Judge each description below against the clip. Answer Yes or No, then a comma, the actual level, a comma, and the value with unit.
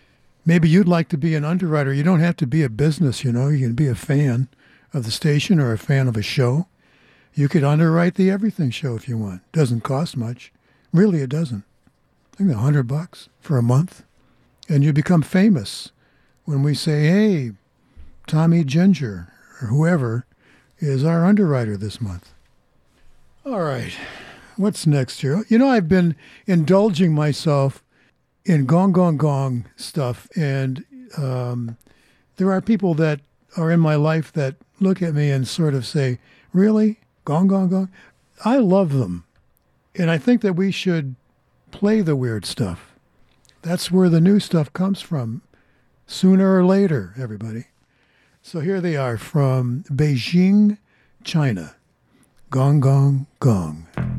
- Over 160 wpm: No, average, 155 wpm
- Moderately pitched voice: Yes, medium, 150 Hz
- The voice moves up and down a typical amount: No, wide, 5.8 semitones